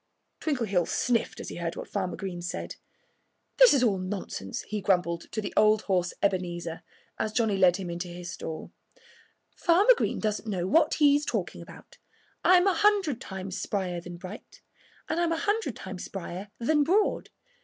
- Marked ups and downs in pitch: Yes, wide, 8.6 semitones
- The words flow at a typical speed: Yes, average, 170 wpm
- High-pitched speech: Yes, high, 200 Hz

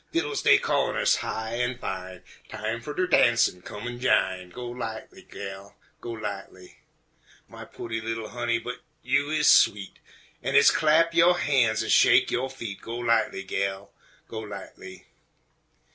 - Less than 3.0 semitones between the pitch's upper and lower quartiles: No, average, 4.2 semitones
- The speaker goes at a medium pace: Yes, average, 155 wpm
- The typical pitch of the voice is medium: No, low, 115 Hz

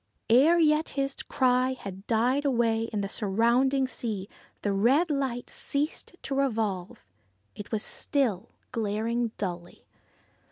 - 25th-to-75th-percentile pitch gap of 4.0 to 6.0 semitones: Yes, average, 4.4 semitones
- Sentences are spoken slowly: Yes, slow, 125 wpm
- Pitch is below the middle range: No, high, 235 Hz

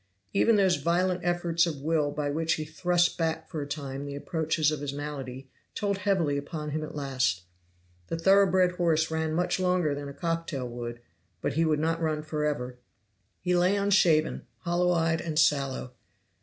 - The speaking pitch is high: No, medium, 160 Hz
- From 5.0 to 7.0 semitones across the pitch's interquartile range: No, average, 3.4 semitones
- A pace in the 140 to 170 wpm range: No, average, 180 wpm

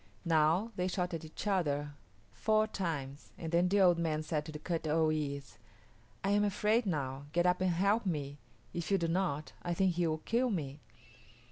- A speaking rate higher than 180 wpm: Yes, average, 195 wpm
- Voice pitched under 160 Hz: No, medium, 170 Hz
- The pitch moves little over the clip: No, average, 3.8 semitones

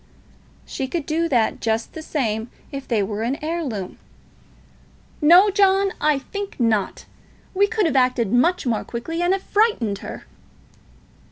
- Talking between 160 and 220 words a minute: No, average, 150 wpm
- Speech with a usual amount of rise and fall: No, wide, 7.7 semitones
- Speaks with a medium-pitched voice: No, very high, 285 Hz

